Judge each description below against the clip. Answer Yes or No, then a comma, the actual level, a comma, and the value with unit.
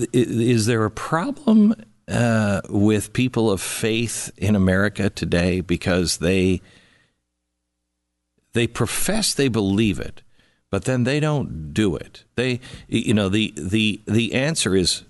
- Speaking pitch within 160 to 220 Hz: No, low, 105 Hz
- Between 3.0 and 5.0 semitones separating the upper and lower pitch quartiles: Yes, average, 4.3 semitones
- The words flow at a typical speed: No, slow, 130 wpm